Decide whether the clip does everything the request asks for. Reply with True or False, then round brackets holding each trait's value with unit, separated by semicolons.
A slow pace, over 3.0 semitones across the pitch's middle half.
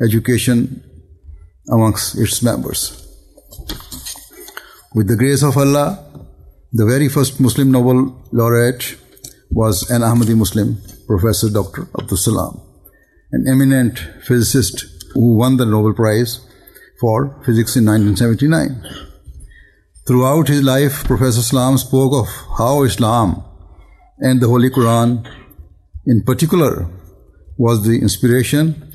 True (110 wpm; 4.1 semitones)